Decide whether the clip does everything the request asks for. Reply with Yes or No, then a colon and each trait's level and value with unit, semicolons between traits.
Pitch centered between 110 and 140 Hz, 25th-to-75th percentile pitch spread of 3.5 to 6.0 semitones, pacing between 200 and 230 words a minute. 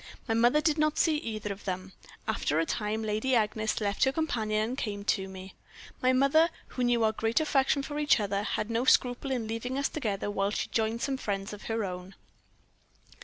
No: high, 225 Hz; average, 4.3 semitones; fast, 205 wpm